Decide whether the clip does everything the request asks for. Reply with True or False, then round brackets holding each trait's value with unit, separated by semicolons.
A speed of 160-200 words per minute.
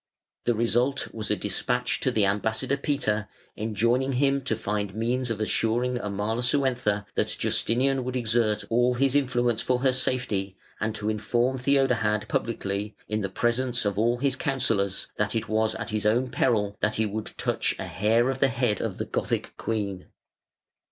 True (165 wpm)